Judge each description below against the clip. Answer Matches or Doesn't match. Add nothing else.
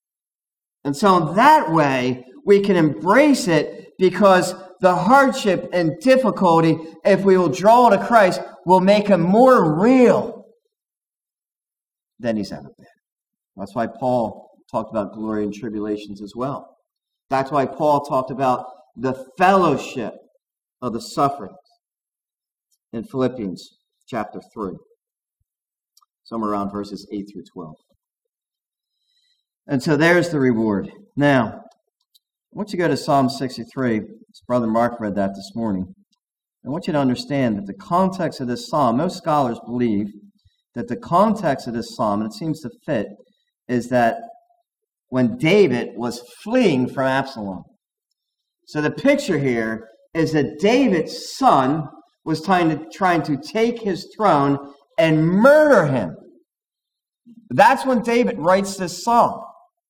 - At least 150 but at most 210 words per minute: Doesn't match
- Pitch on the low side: Doesn't match